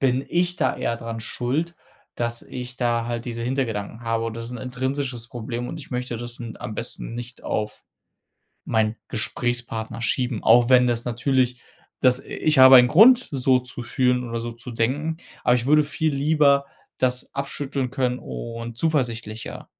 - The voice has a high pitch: No, low, 125 Hz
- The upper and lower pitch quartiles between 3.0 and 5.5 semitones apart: No, narrow, 2.4 semitones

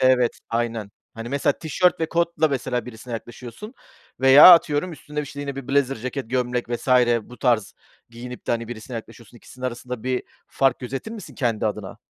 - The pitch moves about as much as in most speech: Yes, average, 3.2 semitones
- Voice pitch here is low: Yes, low, 125 Hz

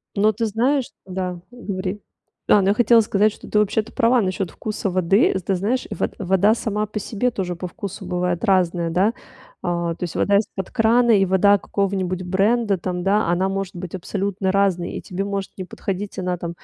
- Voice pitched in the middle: No, high, 195 Hz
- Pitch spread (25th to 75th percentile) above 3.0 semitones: No, narrow, 2.6 semitones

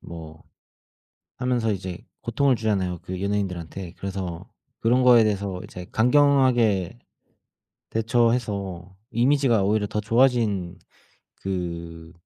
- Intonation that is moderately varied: Yes, average, 4.5 semitones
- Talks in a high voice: No, low, 100 Hz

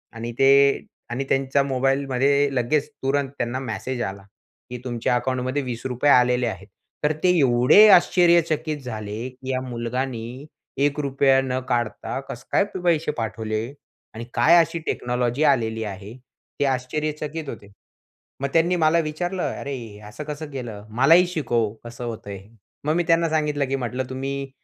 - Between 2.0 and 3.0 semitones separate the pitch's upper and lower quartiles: No, average, 3.8 semitones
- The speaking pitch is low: Yes, low, 130 Hz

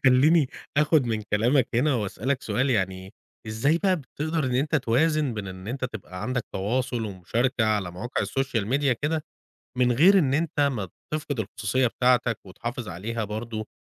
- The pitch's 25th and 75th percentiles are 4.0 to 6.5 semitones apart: Yes, average, 4.6 semitones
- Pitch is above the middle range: No, low, 125 Hz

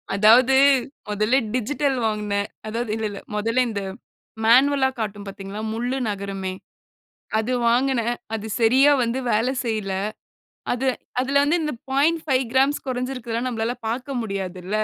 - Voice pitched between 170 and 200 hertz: No, high, 235 Hz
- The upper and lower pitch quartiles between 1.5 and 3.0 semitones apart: No, average, 3.8 semitones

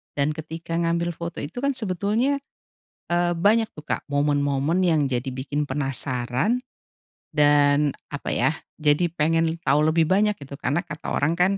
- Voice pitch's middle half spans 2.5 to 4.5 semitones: Yes, average, 3.3 semitones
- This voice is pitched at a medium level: Yes, medium, 155 Hz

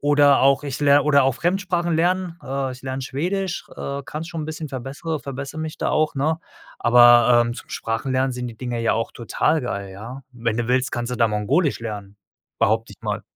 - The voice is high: No, low, 135 Hz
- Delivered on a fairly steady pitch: No, average, 4.5 semitones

